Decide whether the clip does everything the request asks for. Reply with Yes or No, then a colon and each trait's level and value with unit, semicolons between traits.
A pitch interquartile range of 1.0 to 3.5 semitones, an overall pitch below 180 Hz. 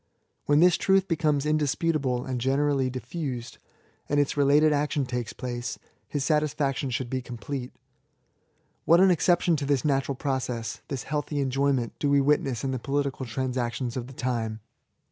Yes: average, 2.7 semitones; low, 135 Hz